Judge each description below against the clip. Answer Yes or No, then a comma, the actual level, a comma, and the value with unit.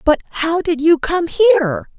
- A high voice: Yes, very high, 330 Hz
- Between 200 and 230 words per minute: No, average, 180 wpm